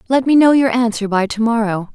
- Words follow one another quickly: Yes, fast, 245 wpm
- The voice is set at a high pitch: Yes, high, 230 Hz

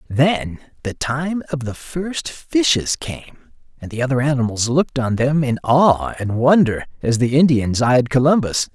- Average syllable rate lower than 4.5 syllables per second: Yes, 4.3 syllables/s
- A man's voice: Yes, male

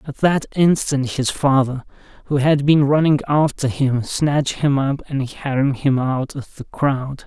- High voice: No, medium, 140 Hz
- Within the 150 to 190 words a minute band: Yes, average, 175 wpm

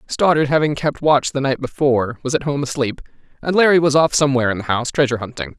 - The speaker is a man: Yes, male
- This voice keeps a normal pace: No, fast, 225 wpm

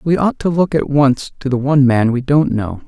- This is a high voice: No, low, 135 Hz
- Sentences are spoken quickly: Yes, fast, 270 wpm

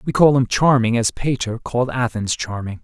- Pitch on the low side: Yes, low, 120 Hz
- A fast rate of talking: No, average, 190 wpm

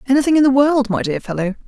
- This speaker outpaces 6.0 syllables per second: Yes, 7.0 syllables/s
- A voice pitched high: Yes, very high, 250 Hz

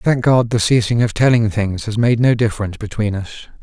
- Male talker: Yes, male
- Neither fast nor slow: No, fast, 215 wpm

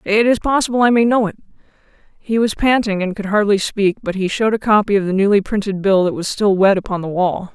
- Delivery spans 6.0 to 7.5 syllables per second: Yes, 6.1 syllables/s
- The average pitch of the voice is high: Yes, high, 205 Hz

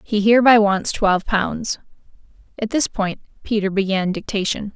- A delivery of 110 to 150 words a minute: Yes, average, 140 wpm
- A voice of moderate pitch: No, high, 205 Hz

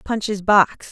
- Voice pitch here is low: No, high, 205 Hz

